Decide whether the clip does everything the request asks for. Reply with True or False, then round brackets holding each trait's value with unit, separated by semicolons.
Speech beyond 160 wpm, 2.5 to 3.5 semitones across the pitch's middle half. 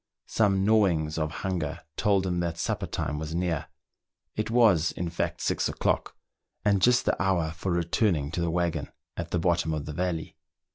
True (180 wpm; 3.1 semitones)